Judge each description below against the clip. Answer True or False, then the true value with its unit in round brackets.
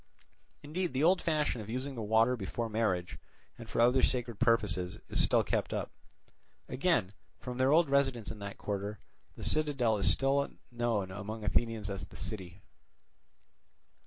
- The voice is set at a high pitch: False (115 Hz)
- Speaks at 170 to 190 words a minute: False (160 wpm)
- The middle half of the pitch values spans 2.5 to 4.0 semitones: False (4.4 semitones)